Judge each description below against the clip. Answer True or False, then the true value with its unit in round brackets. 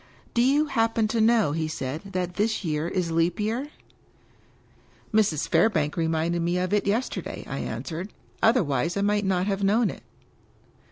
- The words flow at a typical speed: True (185 wpm)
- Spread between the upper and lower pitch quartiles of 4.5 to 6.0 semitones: True (4.9 semitones)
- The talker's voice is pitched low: False (190 Hz)